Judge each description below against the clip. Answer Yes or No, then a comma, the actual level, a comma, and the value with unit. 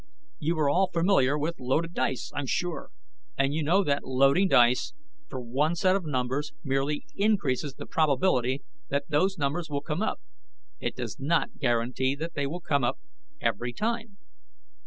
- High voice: No, medium, 145 Hz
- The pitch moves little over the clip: No, average, 4.2 semitones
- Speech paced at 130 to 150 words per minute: No, average, 165 wpm